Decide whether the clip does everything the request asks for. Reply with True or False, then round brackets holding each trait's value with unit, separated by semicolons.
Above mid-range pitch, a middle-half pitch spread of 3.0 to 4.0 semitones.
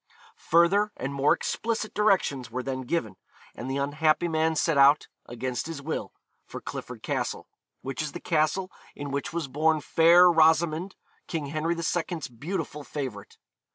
False (155 Hz; 3.6 semitones)